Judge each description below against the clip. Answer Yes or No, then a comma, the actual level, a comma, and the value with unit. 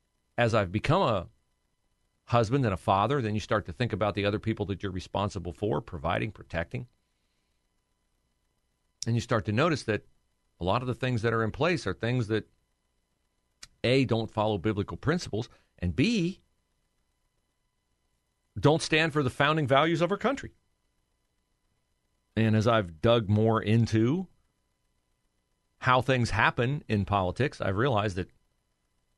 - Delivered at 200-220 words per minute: No, average, 145 wpm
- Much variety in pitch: No, average, 4.1 semitones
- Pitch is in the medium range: No, low, 110 Hz